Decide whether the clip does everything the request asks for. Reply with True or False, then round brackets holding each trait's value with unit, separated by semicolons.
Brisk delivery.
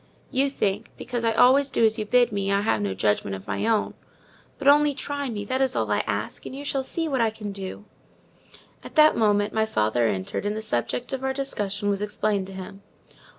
True (215 wpm)